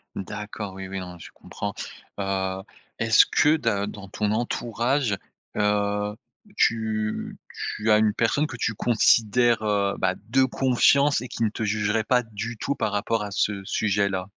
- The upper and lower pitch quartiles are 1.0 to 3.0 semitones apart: Yes, narrow, 2.4 semitones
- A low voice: Yes, low, 105 Hz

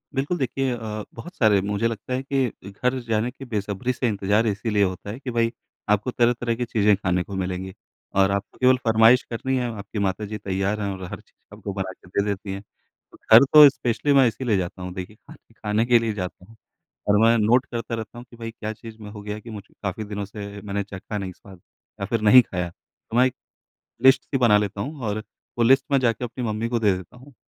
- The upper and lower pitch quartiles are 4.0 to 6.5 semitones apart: No, average, 3.3 semitones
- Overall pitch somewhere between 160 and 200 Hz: No, low, 110 Hz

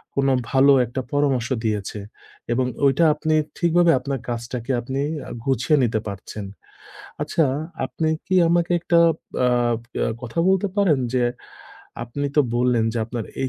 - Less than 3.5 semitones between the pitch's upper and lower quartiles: No, average, 4.7 semitones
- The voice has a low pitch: Yes, low, 130 Hz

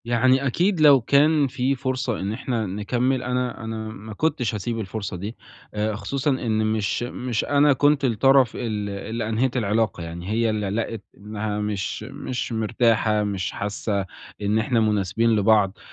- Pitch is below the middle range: Yes, low, 110 Hz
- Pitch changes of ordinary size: Yes, average, 3.4 semitones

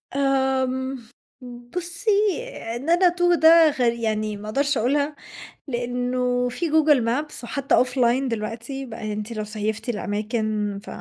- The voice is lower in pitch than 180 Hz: No, very high, 250 Hz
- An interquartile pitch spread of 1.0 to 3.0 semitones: No, average, 3.9 semitones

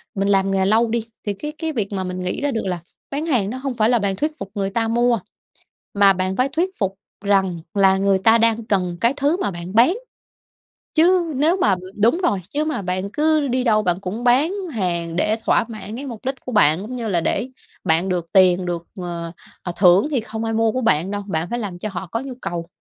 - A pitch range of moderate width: Yes, average, 5.0 semitones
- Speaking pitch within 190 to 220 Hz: Yes, high, 210 Hz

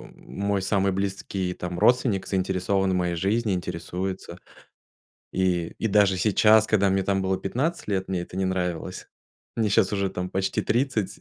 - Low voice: Yes, very low, 95 Hz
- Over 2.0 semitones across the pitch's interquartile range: No, narrow, 1.7 semitones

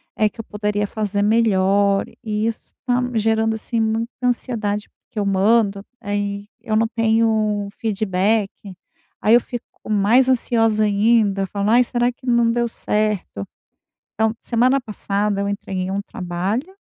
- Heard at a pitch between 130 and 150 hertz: No, high, 215 Hz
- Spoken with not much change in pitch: Yes, narrow, 2.3 semitones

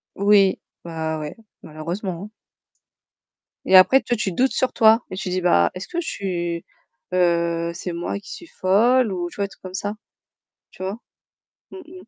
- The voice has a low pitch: No, medium, 185 Hz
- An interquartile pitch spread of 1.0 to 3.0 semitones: No, average, 3.6 semitones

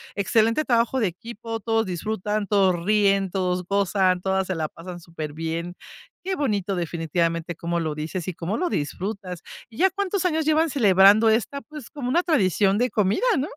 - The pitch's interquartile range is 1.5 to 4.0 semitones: No, average, 4.8 semitones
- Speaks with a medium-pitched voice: No, high, 200 Hz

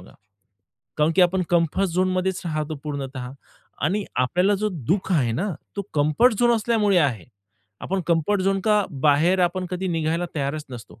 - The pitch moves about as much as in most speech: Yes, average, 4.3 semitones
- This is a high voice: No, medium, 175 Hz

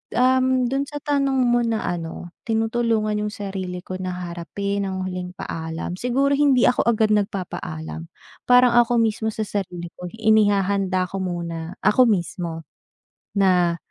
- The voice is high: Yes, high, 200 Hz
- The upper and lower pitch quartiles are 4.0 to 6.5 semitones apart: Yes, average, 4.7 semitones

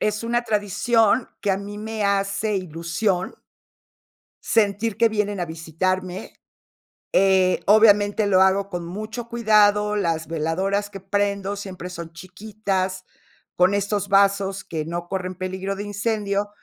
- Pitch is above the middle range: Yes, high, 200 Hz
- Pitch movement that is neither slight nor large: No, narrow, 2.0 semitones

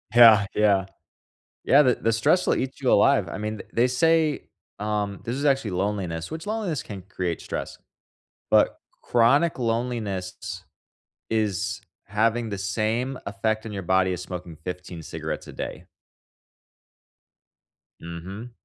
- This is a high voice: No, low, 110 Hz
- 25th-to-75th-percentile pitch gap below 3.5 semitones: No, average, 4.5 semitones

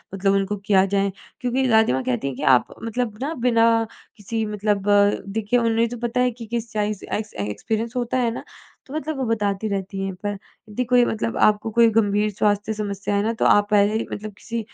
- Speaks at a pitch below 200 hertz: No, high, 215 Hz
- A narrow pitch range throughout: Yes, narrow, 2.3 semitones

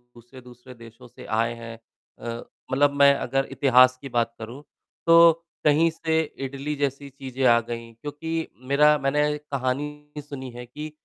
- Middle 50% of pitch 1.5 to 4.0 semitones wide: Yes, average, 3.5 semitones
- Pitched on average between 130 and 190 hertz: Yes, low, 135 Hz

